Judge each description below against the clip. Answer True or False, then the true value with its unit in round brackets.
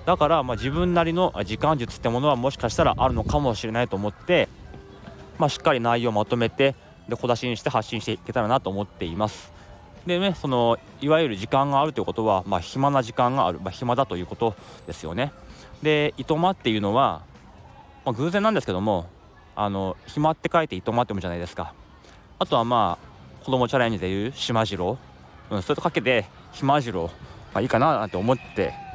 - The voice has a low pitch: True (120 Hz)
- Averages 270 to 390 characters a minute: False (415 characters per minute)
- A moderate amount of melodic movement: False (6.0 semitones)